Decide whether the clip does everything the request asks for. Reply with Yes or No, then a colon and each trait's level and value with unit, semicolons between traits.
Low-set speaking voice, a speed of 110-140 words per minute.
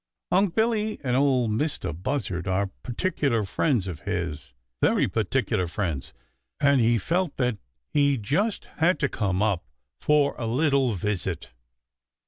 Yes: low, 120 Hz; slow, 135 wpm